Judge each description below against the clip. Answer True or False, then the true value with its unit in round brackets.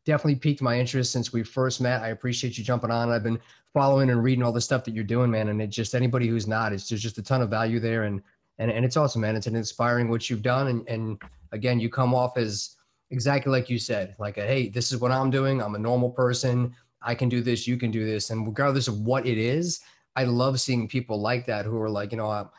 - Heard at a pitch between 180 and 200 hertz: False (120 Hz)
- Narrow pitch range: True (2.2 semitones)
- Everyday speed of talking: False (270 wpm)